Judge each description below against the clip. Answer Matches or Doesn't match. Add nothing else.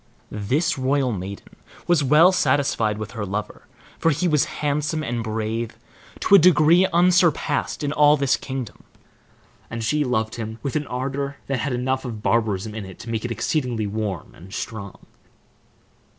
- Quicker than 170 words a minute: Doesn't match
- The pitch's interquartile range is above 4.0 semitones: Matches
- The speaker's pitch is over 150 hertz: Doesn't match